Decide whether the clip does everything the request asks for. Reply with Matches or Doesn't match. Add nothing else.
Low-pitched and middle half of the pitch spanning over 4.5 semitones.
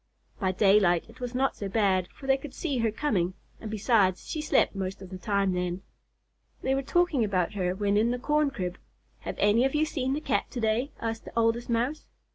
Doesn't match